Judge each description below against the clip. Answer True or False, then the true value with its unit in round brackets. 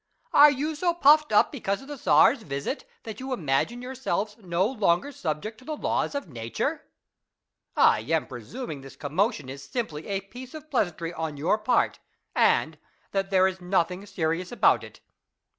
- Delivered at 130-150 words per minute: False (175 wpm)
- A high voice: True (200 Hz)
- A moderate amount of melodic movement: False (8.0 semitones)